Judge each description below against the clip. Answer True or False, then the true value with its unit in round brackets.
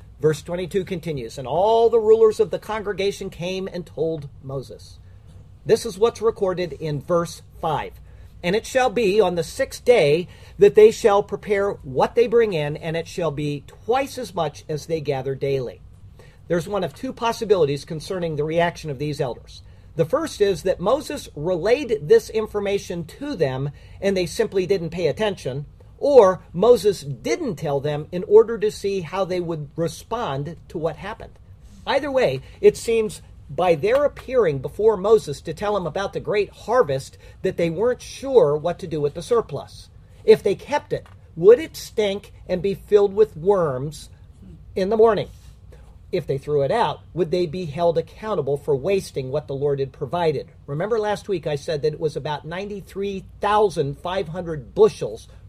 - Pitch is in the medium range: True (180 Hz)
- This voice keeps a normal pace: True (175 wpm)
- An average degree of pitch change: False (6.6 semitones)